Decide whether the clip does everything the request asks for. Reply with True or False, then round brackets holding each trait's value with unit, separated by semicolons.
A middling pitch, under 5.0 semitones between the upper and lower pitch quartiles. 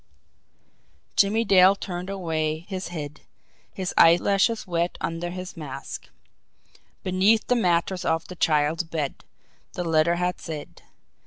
True (175 Hz; 2.6 semitones)